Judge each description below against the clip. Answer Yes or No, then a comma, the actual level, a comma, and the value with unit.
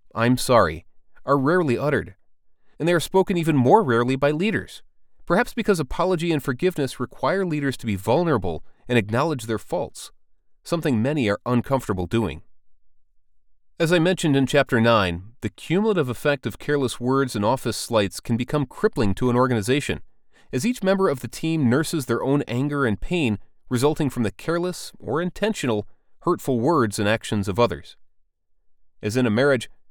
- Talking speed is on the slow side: No, average, 165 wpm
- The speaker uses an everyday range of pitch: No, wide, 5.9 semitones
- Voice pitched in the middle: No, low, 125 Hz